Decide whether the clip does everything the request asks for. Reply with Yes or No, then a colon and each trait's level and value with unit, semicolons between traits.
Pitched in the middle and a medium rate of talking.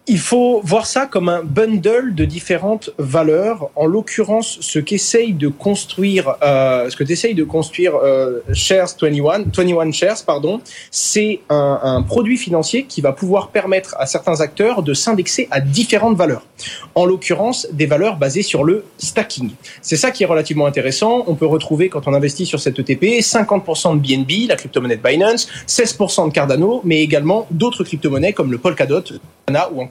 Yes: medium, 175 Hz; average, 175 wpm